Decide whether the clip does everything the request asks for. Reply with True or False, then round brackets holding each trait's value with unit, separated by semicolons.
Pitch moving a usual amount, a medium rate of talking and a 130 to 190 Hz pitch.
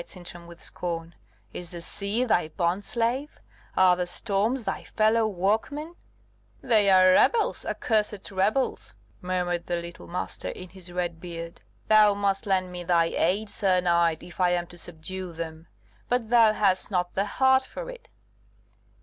True (3.6 semitones; 160 wpm; 185 Hz)